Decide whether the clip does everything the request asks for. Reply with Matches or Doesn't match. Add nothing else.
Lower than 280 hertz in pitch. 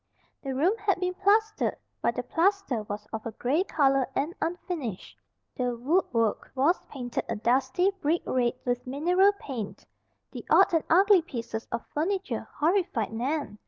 Doesn't match